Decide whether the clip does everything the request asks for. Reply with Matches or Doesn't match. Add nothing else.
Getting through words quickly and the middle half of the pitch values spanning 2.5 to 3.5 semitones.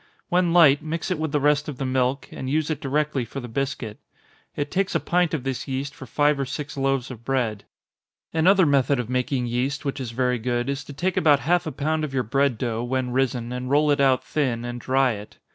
Matches